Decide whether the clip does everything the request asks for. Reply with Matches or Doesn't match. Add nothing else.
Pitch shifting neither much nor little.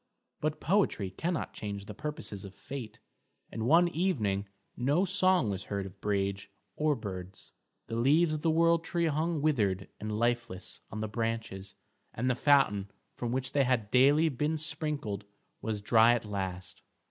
Doesn't match